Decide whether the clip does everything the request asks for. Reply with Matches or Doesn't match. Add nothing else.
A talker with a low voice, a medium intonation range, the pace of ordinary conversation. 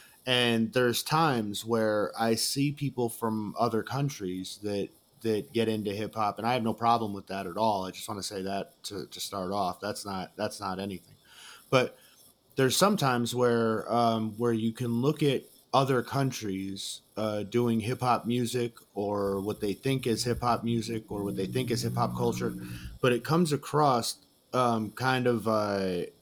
Matches